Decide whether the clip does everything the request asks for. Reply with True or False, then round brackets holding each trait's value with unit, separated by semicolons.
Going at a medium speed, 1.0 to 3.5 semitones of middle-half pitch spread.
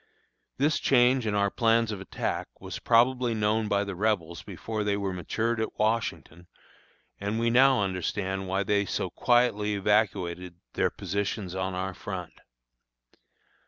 True (145 wpm; 3.1 semitones)